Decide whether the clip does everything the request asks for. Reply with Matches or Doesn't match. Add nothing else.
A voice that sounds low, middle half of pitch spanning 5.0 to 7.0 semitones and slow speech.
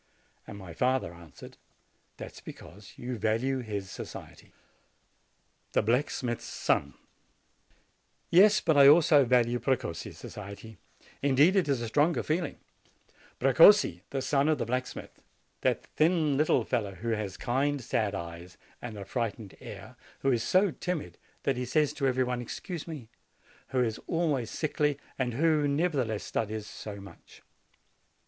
Doesn't match